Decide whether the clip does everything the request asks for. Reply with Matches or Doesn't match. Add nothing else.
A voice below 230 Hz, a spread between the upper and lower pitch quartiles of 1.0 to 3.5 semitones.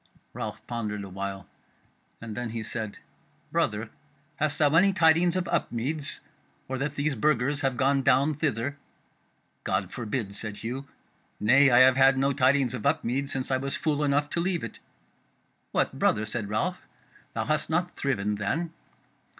Doesn't match